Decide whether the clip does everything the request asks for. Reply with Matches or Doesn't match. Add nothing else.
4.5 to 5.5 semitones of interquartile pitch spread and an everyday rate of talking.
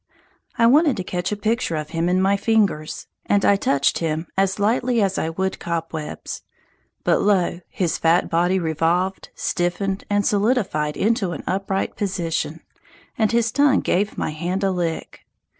Doesn't match